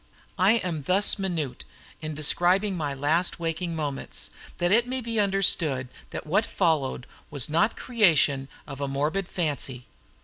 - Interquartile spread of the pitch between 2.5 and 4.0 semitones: No, average, 5.1 semitones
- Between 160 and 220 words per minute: No, average, 145 wpm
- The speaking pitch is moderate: Yes, medium, 165 Hz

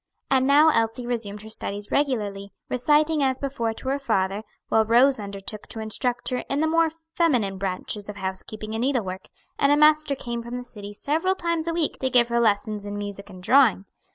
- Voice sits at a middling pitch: No, high, 235 Hz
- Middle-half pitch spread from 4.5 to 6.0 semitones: Yes, average, 5.3 semitones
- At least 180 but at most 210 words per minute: Yes, average, 200 wpm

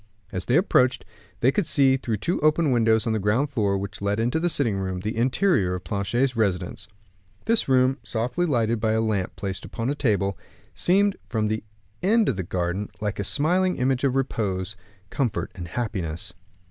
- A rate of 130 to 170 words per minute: No, average, 185 wpm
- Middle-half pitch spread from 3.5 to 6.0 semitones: Yes, average, 5.3 semitones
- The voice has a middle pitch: No, low, 115 Hz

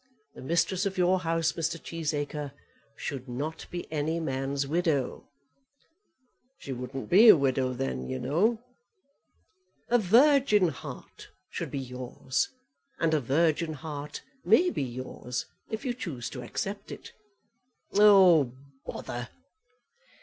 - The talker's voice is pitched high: No, medium, 155 Hz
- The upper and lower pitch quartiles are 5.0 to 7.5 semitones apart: Yes, wide, 5.5 semitones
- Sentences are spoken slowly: Yes, slow, 125 wpm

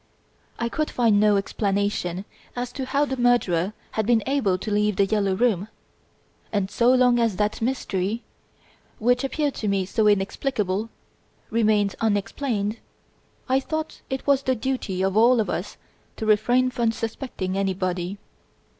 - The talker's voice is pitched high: Yes, high, 220 Hz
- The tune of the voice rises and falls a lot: No, average, 3.8 semitones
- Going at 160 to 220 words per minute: No, average, 150 wpm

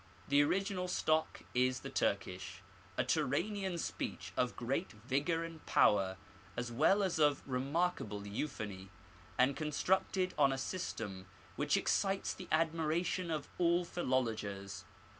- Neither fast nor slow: No, slow, 125 wpm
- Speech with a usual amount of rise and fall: No, wide, 6.6 semitones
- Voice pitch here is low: No, medium, 145 Hz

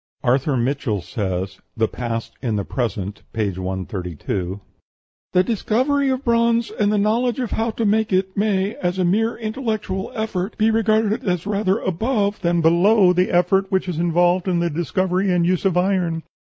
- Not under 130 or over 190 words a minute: Yes, average, 170 wpm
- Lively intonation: Yes, wide, 5.9 semitones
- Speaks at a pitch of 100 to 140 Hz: No, medium, 185 Hz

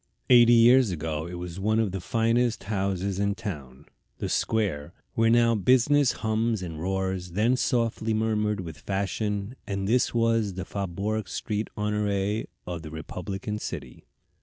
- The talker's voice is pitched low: Yes, low, 105 Hz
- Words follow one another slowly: No, average, 150 wpm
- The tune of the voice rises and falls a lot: No, average, 3.6 semitones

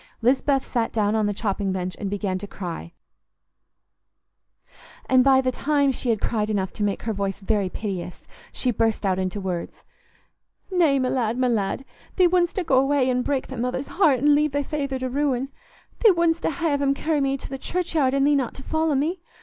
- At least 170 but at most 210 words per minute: Yes, average, 200 wpm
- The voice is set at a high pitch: Yes, very high, 260 Hz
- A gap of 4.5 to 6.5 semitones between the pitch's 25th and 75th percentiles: Yes, wide, 5.6 semitones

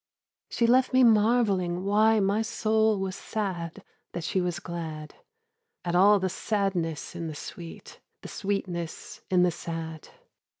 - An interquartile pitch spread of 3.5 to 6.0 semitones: Yes, average, 3.8 semitones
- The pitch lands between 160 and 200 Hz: Yes, high, 190 Hz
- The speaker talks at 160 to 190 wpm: No, average, 140 wpm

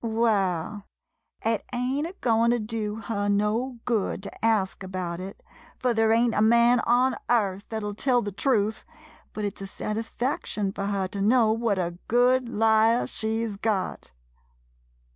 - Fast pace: No, average, 170 wpm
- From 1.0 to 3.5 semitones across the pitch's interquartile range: Yes, average, 2.7 semitones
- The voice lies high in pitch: Yes, high, 220 Hz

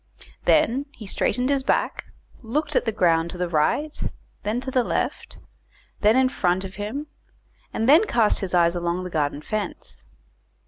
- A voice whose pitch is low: No, high, 210 Hz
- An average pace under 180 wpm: Yes, average, 170 wpm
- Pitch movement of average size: No, wide, 6.6 semitones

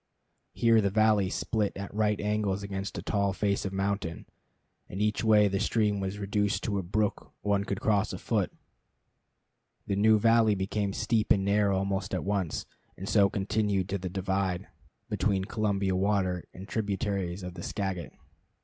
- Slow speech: No, average, 165 wpm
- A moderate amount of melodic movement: No, narrow, 1.5 semitones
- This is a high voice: No, low, 100 Hz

